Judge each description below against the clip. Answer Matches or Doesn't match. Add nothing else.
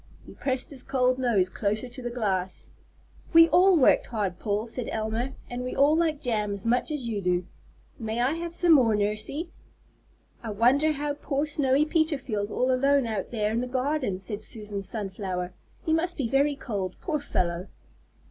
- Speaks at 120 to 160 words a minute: Doesn't match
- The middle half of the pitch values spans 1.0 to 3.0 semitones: Doesn't match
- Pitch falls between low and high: Doesn't match